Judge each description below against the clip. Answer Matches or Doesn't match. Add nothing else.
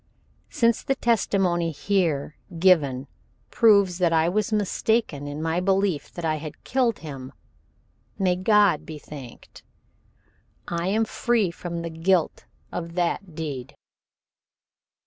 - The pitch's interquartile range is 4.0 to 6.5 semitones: Matches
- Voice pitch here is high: Doesn't match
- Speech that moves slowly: Matches